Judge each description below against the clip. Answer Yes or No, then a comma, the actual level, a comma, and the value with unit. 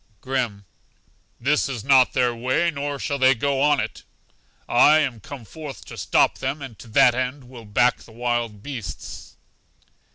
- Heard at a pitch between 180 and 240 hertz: No, low, 130 Hz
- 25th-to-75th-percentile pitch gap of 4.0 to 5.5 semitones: No, average, 3.1 semitones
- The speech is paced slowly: No, average, 165 wpm